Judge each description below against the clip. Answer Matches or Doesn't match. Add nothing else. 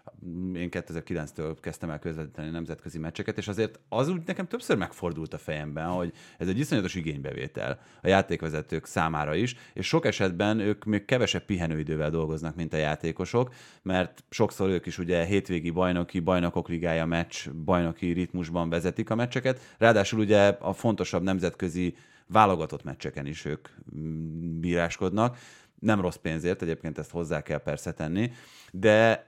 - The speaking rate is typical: Matches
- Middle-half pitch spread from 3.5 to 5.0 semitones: Matches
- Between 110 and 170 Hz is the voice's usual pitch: Doesn't match